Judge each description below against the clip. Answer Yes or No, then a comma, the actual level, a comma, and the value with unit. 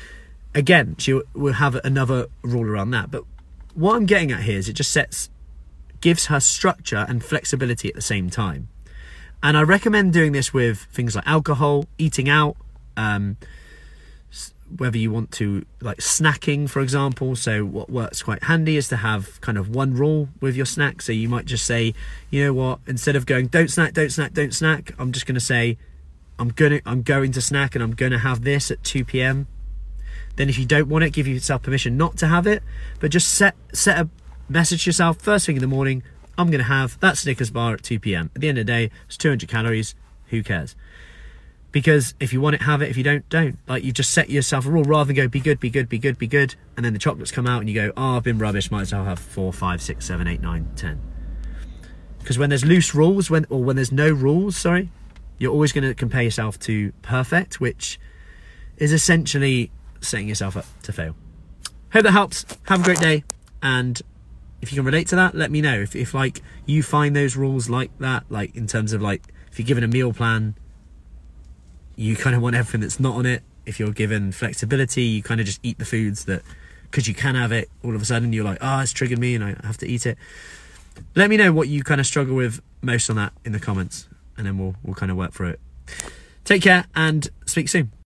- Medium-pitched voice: No, low, 125 Hz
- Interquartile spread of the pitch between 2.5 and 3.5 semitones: No, wide, 5.5 semitones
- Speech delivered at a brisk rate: Yes, fast, 230 wpm